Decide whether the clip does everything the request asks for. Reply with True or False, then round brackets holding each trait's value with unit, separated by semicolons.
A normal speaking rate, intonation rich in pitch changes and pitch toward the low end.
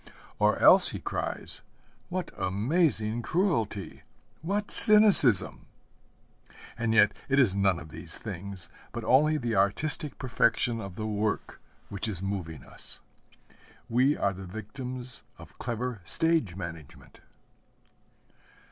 False (120 wpm; 5.8 semitones; 110 Hz)